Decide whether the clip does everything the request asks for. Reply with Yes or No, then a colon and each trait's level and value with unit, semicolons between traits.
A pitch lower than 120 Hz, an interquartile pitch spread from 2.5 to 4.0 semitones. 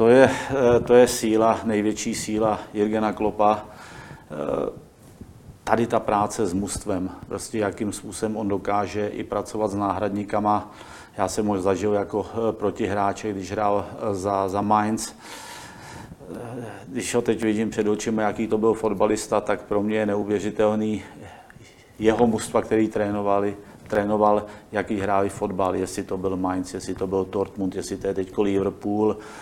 No: low, 105 Hz; narrow, 1.6 semitones